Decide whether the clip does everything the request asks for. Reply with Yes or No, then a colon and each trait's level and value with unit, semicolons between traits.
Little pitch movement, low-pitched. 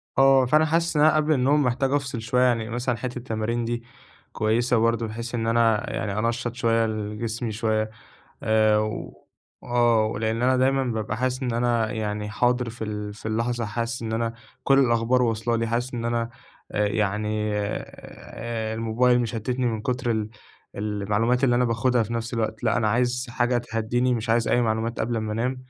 Yes: narrow, 2.0 semitones; low, 115 Hz